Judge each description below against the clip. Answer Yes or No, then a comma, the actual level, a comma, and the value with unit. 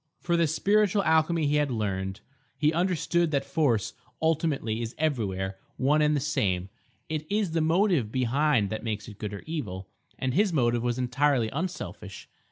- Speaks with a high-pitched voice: No, medium, 140 Hz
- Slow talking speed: No, average, 170 wpm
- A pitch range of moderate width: No, wide, 6.7 semitones